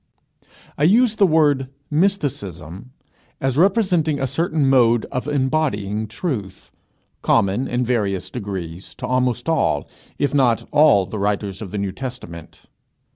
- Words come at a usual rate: No, slow, 130 wpm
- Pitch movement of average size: No, wide, 6.9 semitones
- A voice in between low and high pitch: No, low, 125 Hz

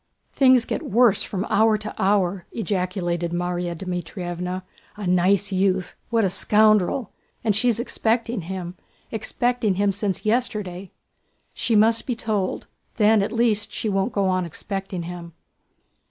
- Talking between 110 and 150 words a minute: Yes, slow, 135 wpm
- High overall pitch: Yes, high, 200 Hz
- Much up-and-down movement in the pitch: No, average, 3.3 semitones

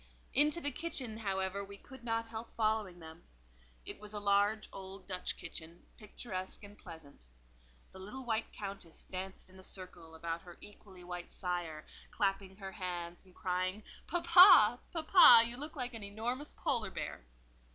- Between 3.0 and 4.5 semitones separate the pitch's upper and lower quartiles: Yes, average, 3.8 semitones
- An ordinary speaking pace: Yes, average, 160 wpm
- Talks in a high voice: Yes, high, 200 Hz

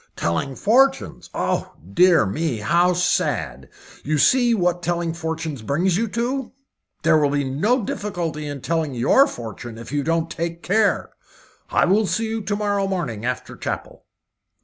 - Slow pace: No, average, 155 wpm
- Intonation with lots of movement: Yes, wide, 6.1 semitones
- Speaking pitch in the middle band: Yes, medium, 170 Hz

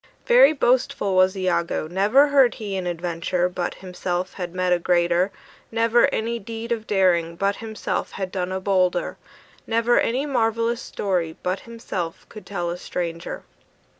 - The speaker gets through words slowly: No, average, 155 wpm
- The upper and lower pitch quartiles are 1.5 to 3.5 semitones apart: No, average, 4.3 semitones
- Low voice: No, high, 190 Hz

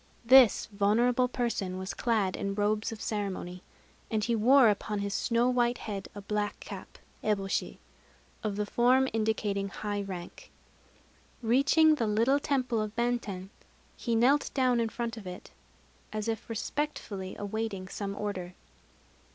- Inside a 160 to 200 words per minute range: No, average, 145 wpm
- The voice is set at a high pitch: Yes, high, 215 Hz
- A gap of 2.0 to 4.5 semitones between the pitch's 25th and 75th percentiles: Yes, average, 3.1 semitones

